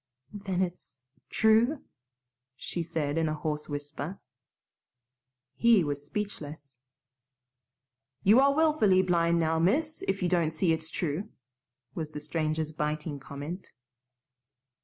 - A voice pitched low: No, medium, 165 Hz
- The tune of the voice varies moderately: Yes, average, 4.5 semitones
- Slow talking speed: Yes, slow, 115 wpm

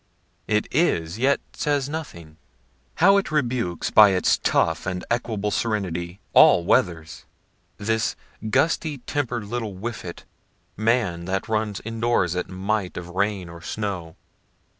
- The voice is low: Yes, low, 105 Hz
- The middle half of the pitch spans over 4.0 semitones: Yes, average, 5.0 semitones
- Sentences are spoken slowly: Yes, slow, 130 wpm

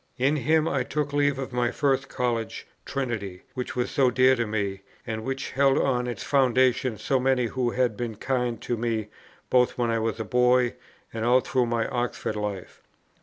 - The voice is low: Yes, low, 125 Hz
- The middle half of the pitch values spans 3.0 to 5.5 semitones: No, narrow, 2.5 semitones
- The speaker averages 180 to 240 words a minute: Yes, average, 190 wpm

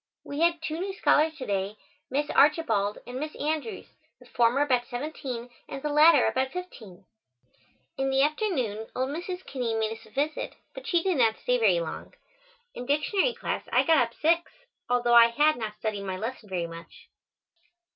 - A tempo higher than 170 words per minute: Yes, average, 180 wpm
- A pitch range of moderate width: No, wide, 5.7 semitones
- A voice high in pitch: Yes, very high, 265 Hz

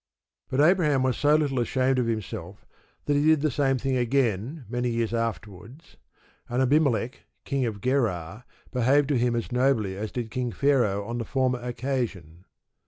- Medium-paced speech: Yes, average, 170 wpm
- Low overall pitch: Yes, low, 125 Hz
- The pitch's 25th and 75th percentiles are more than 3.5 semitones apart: No, average, 3.2 semitones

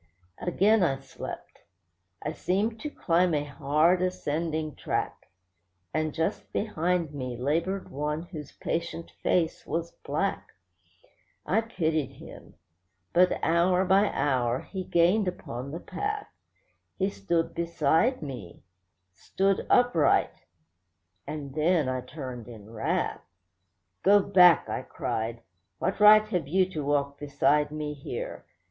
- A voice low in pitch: No, medium, 160 Hz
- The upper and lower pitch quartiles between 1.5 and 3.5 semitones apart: No, average, 4.6 semitones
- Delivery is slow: Yes, slow, 120 wpm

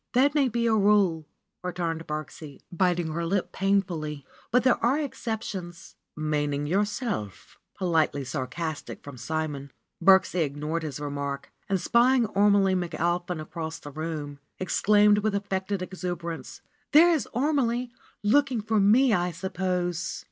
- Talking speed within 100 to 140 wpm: Yes, slow, 135 wpm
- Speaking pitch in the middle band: Yes, medium, 180 Hz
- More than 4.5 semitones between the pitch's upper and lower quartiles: Yes, average, 4.9 semitones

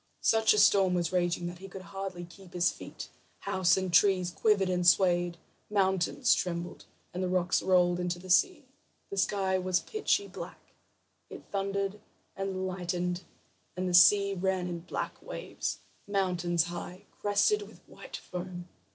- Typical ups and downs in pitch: No, narrow, 1.8 semitones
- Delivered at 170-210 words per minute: No, average, 155 wpm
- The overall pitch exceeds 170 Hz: Yes, medium, 185 Hz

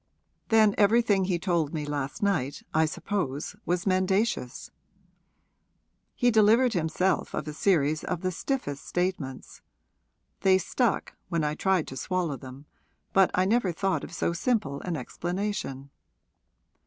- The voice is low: No, medium, 180 Hz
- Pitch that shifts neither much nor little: Yes, average, 4.9 semitones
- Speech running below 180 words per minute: Yes, slow, 135 wpm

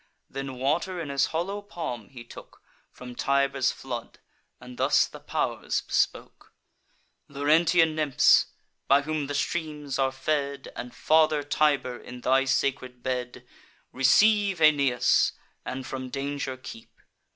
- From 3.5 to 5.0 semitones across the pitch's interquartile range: No, average, 3.1 semitones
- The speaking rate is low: Yes, slow, 130 wpm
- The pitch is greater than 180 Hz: No, medium, 140 Hz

